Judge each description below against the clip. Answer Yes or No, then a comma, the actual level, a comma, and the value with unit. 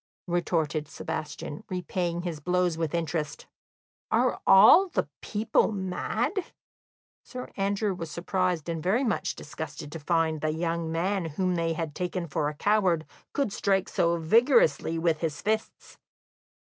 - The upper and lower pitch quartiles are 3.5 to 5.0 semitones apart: No, average, 3.1 semitones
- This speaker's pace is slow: No, average, 145 wpm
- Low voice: No, medium, 170 Hz